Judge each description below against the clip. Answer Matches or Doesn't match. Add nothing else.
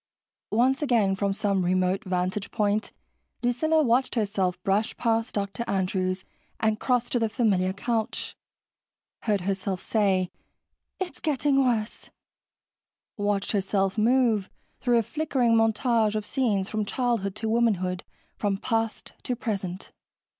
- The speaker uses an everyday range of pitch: Matches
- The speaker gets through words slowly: Matches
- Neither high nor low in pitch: Doesn't match